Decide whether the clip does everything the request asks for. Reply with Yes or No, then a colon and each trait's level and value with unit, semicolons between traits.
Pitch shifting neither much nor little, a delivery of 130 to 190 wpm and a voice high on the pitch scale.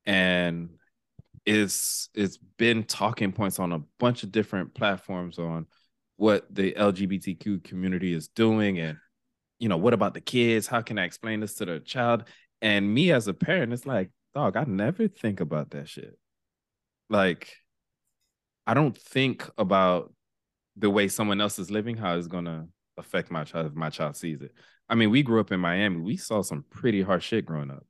No: average, 4.2 semitones; average, 185 wpm; low, 100 Hz